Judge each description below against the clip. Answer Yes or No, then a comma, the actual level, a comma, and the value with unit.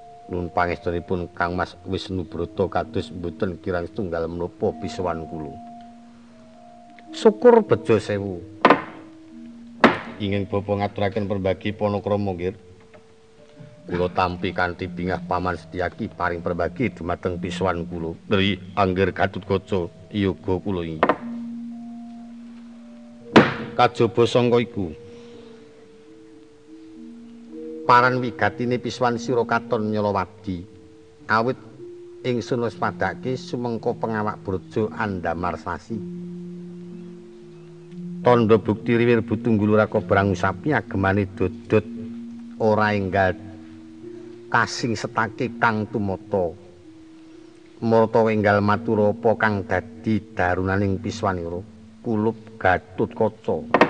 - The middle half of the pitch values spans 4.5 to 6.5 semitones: Yes, average, 5.3 semitones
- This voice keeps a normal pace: Yes, average, 95 wpm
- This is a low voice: Yes, low, 110 Hz